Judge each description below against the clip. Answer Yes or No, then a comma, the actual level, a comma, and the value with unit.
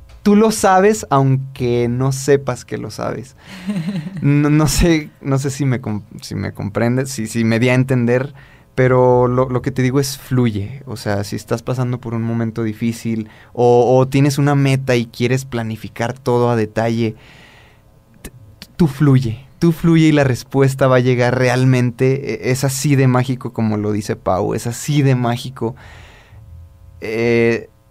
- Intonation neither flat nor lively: Yes, average, 3.0 semitones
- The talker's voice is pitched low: Yes, low, 125 Hz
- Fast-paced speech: No, average, 170 wpm